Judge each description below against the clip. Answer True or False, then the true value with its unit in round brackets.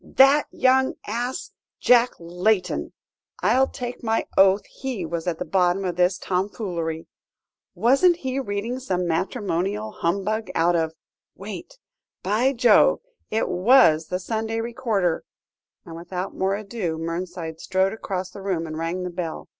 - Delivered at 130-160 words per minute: True (140 wpm)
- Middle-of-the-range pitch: False (195 Hz)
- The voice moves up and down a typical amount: True (4.9 semitones)